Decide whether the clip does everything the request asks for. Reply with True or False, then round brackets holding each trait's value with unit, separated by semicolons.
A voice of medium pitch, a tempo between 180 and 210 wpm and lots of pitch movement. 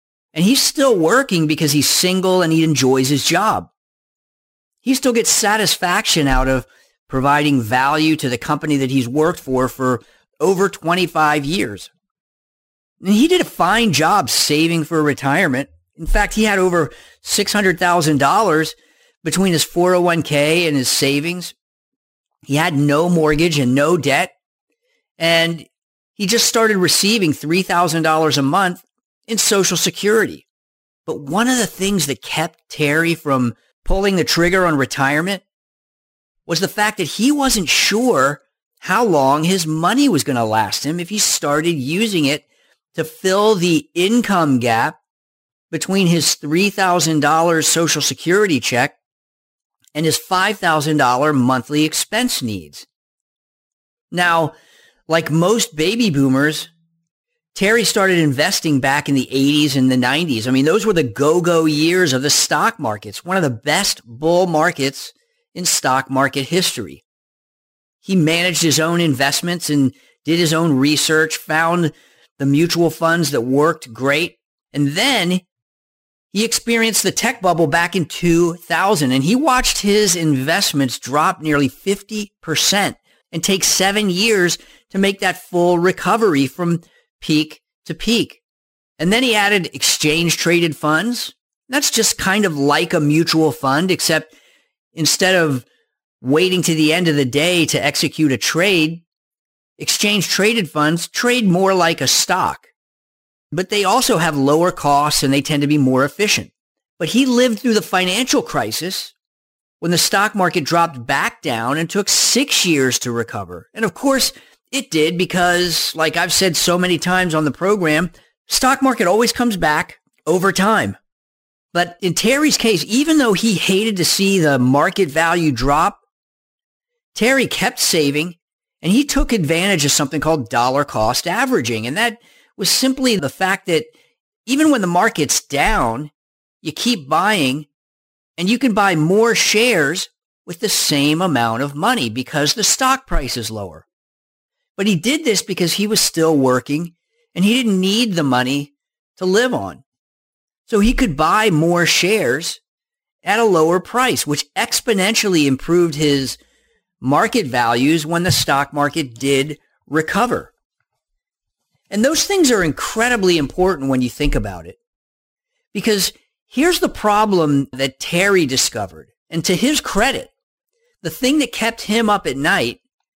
False (170 Hz; 150 wpm; 5.8 semitones)